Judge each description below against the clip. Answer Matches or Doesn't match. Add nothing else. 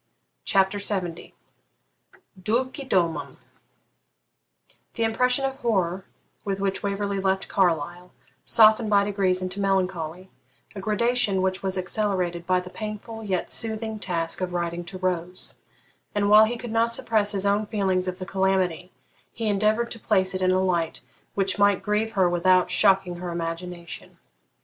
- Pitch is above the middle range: Matches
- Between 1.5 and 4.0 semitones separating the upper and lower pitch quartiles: Matches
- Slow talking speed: Doesn't match